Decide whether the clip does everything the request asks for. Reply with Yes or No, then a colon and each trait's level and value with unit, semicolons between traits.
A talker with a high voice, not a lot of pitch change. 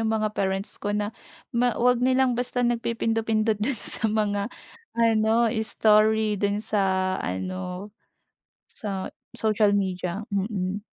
Yes: high, 215 Hz; narrow, 2.3 semitones